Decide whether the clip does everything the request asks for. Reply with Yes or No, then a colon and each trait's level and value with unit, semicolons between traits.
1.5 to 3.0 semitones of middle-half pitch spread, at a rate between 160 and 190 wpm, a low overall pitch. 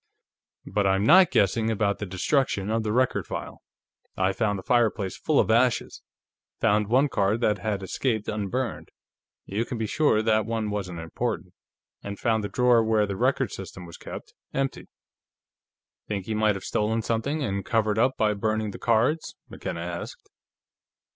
Yes: narrow, 2.6 semitones; average, 170 wpm; low, 110 Hz